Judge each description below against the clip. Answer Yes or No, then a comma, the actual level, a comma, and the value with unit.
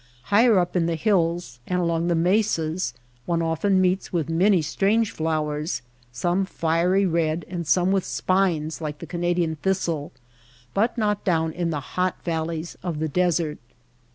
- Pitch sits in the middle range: Yes, medium, 170 Hz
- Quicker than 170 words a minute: No, average, 155 wpm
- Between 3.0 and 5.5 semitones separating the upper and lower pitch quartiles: No, narrow, 2.6 semitones